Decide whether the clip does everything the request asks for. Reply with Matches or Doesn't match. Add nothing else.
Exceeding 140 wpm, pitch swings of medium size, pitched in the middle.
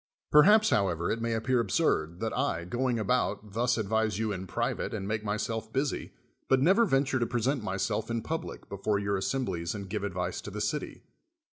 Doesn't match